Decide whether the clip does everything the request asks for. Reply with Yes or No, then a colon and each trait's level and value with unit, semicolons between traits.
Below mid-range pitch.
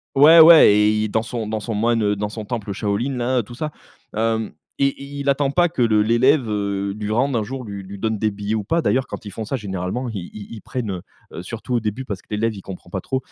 Yes: low, 110 Hz